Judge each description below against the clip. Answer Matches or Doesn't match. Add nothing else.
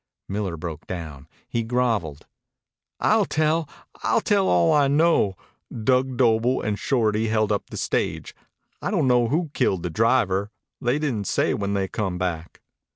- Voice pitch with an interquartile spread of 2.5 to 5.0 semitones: Doesn't match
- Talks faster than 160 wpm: Doesn't match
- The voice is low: Matches